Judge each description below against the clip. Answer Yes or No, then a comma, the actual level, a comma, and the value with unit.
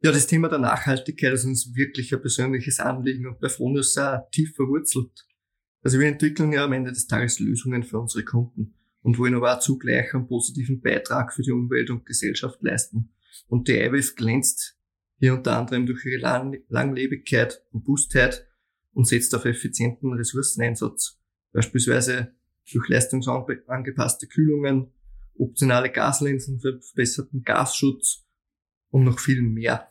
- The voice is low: Yes, low, 130 Hz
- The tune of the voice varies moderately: No, narrow, 2.1 semitones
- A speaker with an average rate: Yes, average, 145 wpm